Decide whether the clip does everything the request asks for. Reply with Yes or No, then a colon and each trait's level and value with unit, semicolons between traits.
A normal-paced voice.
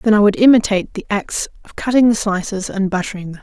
No: fast, 230 wpm